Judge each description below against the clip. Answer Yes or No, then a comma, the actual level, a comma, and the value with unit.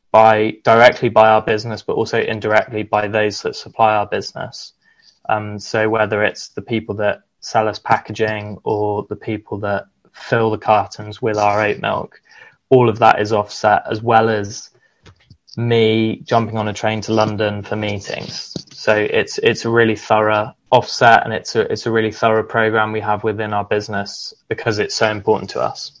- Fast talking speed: No, average, 180 wpm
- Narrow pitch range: Yes, narrow, 1.1 semitones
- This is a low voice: Yes, low, 110 Hz